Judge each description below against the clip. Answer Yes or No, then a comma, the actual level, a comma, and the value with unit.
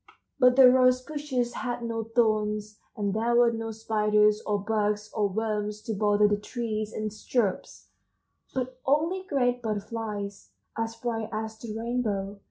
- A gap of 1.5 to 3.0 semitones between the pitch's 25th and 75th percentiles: Yes, narrow, 2.4 semitones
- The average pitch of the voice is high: Yes, high, 220 Hz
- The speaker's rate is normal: Yes, average, 150 wpm